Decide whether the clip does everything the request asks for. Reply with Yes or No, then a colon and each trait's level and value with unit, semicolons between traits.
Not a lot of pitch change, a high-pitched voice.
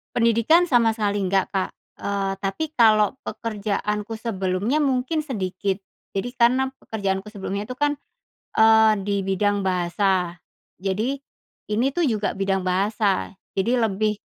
No: average, 3.4 semitones; high, 210 Hz